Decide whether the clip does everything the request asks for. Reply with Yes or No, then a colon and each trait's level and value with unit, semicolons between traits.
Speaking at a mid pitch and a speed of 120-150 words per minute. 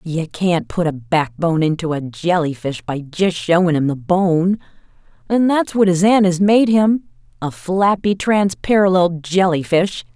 Yes: medium, 175 Hz; average, 140 wpm